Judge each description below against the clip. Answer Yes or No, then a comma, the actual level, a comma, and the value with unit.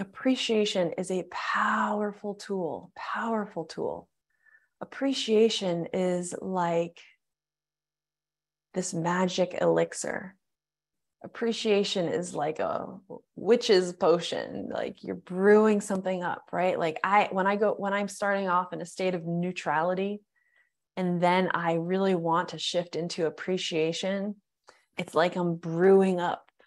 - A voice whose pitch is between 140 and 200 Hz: Yes, medium, 185 Hz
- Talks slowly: Yes, slow, 120 wpm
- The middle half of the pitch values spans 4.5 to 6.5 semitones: No, average, 3.1 semitones